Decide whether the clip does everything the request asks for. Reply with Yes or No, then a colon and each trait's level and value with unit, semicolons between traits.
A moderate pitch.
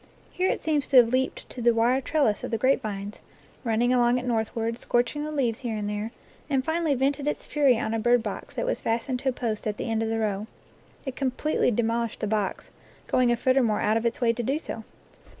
No: high, 240 Hz